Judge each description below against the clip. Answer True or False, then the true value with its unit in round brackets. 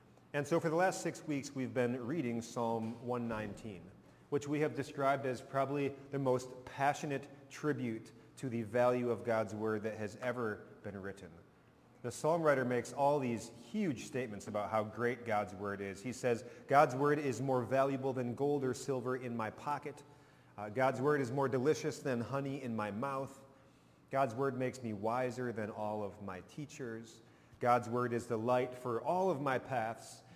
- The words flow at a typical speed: True (180 wpm)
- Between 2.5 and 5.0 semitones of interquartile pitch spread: True (3.3 semitones)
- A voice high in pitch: False (125 Hz)